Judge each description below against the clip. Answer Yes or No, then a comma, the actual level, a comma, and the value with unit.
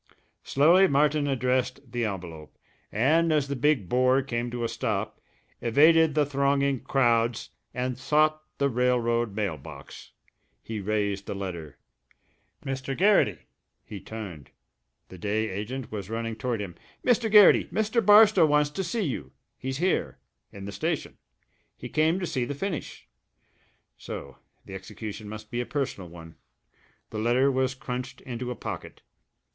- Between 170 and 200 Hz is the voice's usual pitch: No, low, 125 Hz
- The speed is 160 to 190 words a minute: No, average, 150 wpm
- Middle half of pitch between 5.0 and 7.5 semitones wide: Yes, wide, 5.4 semitones